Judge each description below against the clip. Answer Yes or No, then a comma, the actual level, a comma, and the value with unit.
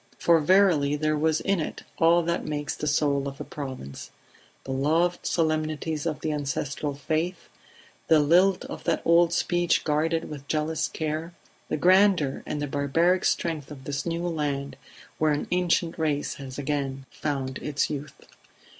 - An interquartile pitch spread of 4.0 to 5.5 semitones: No, average, 2.8 semitones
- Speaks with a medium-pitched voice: Yes, medium, 155 Hz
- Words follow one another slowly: No, average, 160 wpm